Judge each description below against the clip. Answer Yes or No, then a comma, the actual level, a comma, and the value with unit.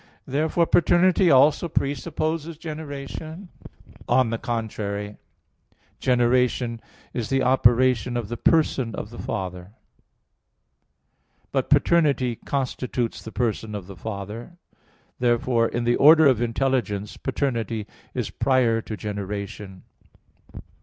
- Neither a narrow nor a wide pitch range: Yes, average, 4.1 semitones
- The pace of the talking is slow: Yes, slow, 105 wpm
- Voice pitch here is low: Yes, low, 120 Hz